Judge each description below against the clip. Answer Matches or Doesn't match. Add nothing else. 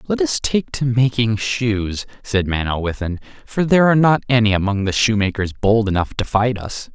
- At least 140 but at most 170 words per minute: Doesn't match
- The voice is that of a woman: Doesn't match